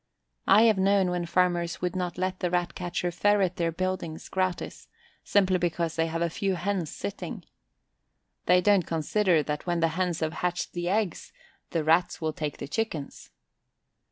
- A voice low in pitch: No, medium, 175 Hz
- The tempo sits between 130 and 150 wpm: No, average, 170 wpm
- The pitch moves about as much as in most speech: No, narrow, 2.1 semitones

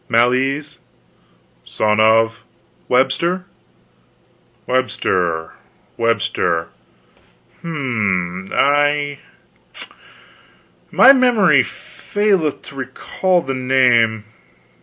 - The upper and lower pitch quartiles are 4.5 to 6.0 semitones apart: Yes, average, 5.2 semitones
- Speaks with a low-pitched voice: Yes, low, 130 Hz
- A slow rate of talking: Yes, slow, 65 wpm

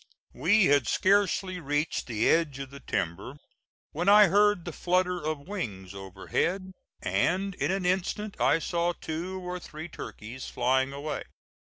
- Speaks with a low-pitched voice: No, medium, 170 Hz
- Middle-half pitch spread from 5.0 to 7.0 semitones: Yes, average, 5.3 semitones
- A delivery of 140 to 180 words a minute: Yes, average, 150 wpm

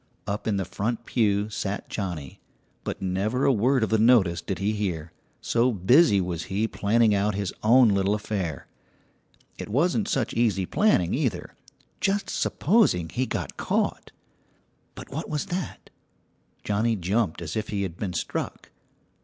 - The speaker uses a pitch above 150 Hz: No, low, 105 Hz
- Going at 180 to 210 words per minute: No, average, 155 wpm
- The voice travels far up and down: No, average, 4.1 semitones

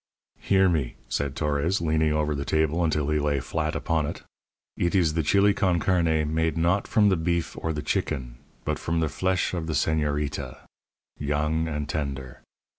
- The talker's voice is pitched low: Yes, very low, 80 Hz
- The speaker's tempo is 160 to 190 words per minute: Yes, average, 180 wpm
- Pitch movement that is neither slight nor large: No, narrow, 2.3 semitones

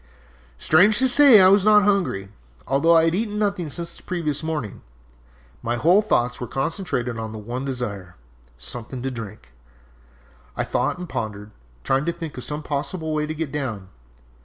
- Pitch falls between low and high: Yes, medium, 150 Hz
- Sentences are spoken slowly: No, average, 175 wpm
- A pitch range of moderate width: No, wide, 7.0 semitones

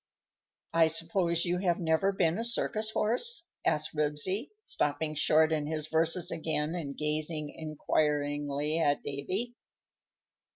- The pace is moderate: No, slow, 130 wpm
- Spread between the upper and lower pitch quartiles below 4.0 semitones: Yes, average, 2.9 semitones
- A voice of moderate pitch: Yes, medium, 160 Hz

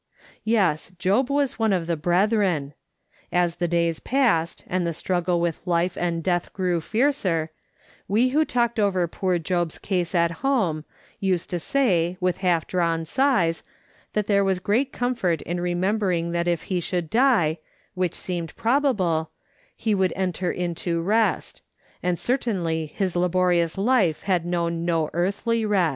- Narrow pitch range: No, average, 3.7 semitones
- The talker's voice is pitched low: No, medium, 180 Hz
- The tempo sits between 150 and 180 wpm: Yes, average, 155 wpm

